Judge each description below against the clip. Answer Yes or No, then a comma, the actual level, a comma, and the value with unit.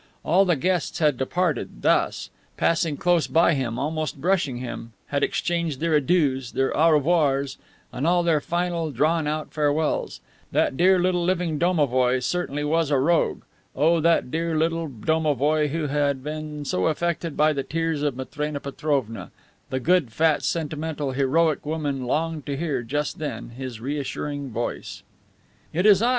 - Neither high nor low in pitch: Yes, medium, 150 Hz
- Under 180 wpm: Yes, average, 160 wpm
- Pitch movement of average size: Yes, average, 3.2 semitones